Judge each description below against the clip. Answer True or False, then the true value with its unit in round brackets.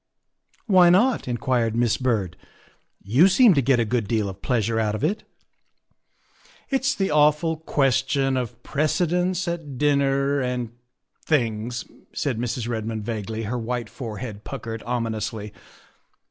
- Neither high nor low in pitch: False (125 Hz)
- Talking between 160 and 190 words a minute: False (150 wpm)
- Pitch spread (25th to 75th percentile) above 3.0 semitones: True (5.0 semitones)